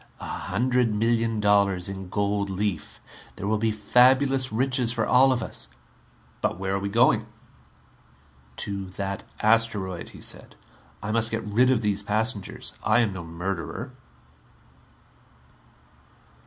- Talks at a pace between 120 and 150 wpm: Yes, average, 140 wpm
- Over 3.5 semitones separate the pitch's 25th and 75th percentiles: No, average, 3.0 semitones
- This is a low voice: Yes, low, 105 Hz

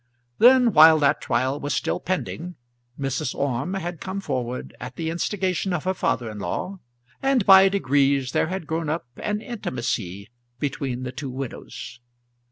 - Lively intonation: Yes, wide, 6.5 semitones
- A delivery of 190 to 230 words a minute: No, average, 160 wpm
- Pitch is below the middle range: No, medium, 150 Hz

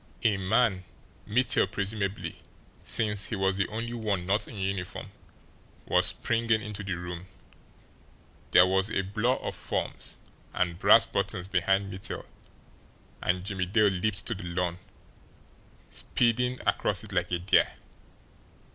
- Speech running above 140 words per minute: No, slow, 135 wpm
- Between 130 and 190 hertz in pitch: No, low, 100 Hz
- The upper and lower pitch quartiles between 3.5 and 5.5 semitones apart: No, average, 2.8 semitones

